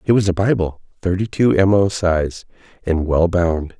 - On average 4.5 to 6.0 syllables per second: No, 4.2 syllables/s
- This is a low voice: Yes, very low, 90 Hz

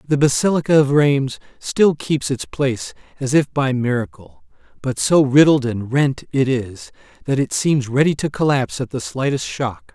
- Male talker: Yes, male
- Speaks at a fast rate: No, average, 175 wpm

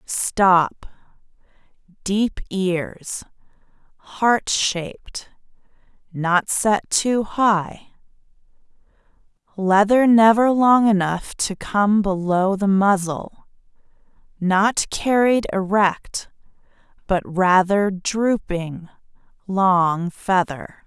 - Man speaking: No, female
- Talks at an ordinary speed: No, slow, 70 wpm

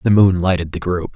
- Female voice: No, male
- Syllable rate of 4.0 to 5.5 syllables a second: No, 5.7 syllables/s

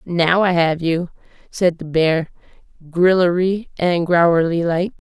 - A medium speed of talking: No, slow, 130 wpm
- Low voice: No, medium, 175 Hz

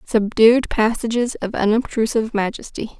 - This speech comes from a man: No, female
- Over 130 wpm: No, slow, 100 wpm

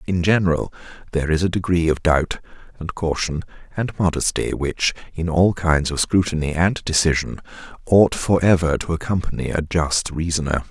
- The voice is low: Yes, very low, 85 Hz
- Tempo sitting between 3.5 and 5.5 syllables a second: Yes, 5.1 syllables/s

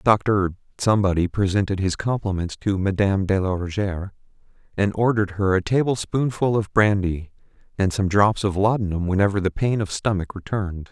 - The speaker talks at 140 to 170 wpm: Yes, average, 160 wpm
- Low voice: Yes, low, 100 Hz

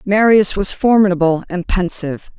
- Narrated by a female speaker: Yes, female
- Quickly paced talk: No, slow, 125 wpm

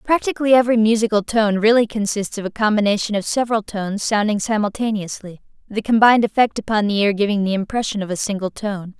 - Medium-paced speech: Yes, average, 180 wpm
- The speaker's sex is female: Yes, female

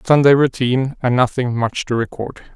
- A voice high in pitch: No, low, 125 Hz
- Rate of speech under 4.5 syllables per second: No, 5.0 syllables/s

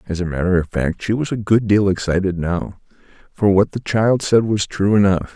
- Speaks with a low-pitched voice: Yes, low, 100 Hz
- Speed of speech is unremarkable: No, fast, 225 wpm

